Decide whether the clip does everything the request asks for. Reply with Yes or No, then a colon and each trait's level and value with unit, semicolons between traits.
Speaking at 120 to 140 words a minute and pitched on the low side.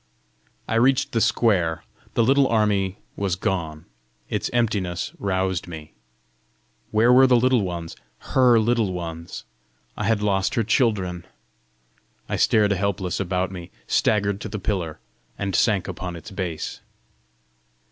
Yes: slow, 135 wpm; low, 100 Hz